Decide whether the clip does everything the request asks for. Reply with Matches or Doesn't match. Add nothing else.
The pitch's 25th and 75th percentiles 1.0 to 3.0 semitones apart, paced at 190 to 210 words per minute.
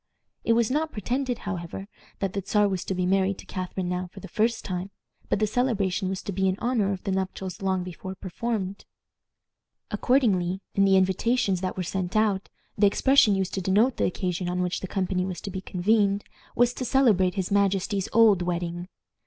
Matches